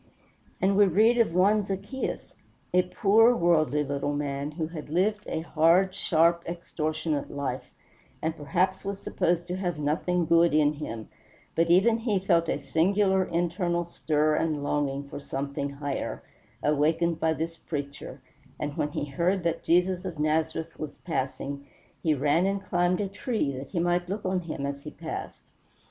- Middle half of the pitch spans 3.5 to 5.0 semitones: Yes, average, 3.9 semitones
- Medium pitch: Yes, medium, 165 Hz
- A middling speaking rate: Yes, average, 165 wpm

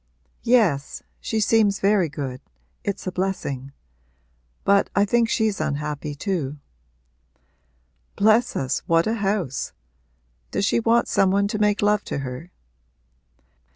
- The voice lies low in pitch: No, high, 195 Hz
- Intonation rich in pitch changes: Yes, wide, 6.1 semitones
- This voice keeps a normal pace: No, slow, 125 wpm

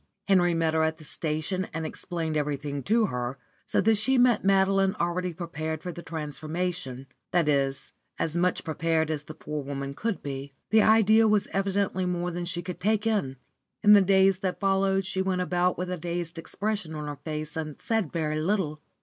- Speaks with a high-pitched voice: No, medium, 175 Hz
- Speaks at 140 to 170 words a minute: No, average, 190 wpm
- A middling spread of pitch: Yes, average, 3.9 semitones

